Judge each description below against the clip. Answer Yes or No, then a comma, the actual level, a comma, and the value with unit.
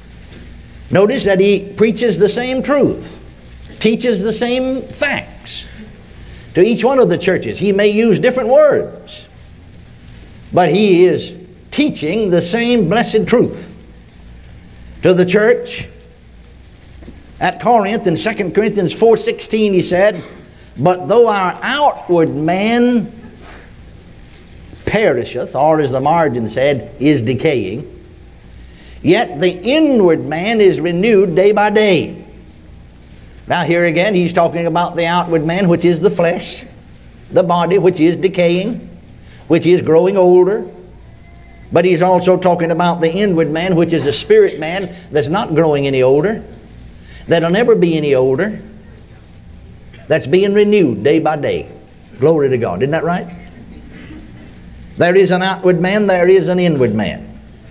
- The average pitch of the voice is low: No, medium, 180 Hz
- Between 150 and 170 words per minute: No, slow, 135 wpm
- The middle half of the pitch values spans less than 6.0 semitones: Yes, wide, 5.6 semitones